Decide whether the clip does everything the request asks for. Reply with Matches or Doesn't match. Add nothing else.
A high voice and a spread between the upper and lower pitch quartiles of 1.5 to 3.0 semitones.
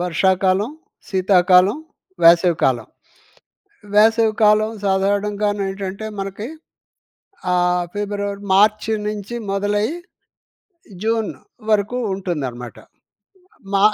Matches